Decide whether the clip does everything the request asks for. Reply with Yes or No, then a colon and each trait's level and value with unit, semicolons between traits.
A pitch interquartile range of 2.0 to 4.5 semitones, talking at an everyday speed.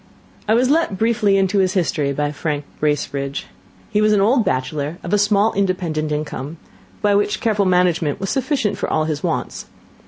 No: wide, 5.5 semitones; average, 180 wpm